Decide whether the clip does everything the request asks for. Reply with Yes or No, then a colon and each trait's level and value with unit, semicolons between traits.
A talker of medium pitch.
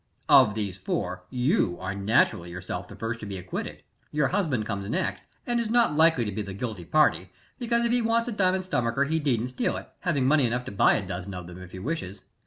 No: low, 115 Hz